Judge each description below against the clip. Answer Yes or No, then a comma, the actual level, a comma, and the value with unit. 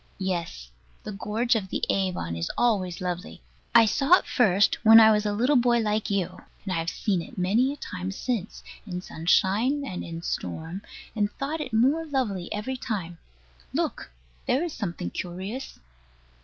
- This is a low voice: No, high, 205 Hz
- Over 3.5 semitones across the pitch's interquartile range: Yes, average, 5.0 semitones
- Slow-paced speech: No, average, 170 wpm